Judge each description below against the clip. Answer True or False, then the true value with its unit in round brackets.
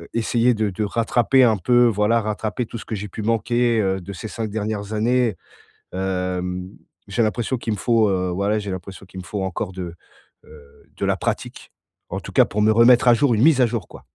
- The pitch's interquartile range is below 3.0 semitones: False (3.5 semitones)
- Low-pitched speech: True (110 Hz)